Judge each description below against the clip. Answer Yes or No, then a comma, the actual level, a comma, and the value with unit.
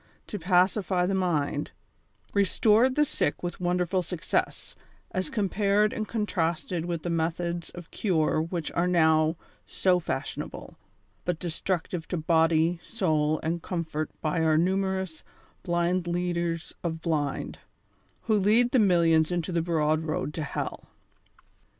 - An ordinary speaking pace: No, slow, 130 wpm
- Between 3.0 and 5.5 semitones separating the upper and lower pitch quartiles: No, narrow, 2.6 semitones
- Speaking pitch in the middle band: Yes, medium, 175 Hz